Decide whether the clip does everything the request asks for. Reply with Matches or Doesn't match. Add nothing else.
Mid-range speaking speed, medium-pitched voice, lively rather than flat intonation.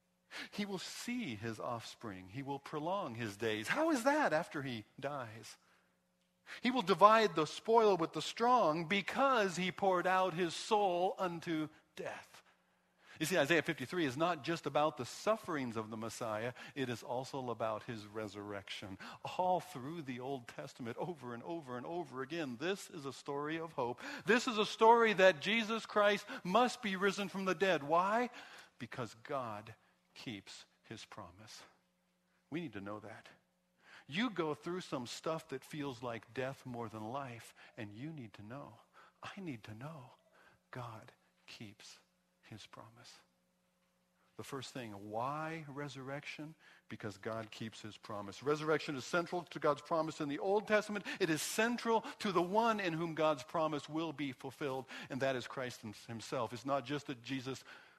Matches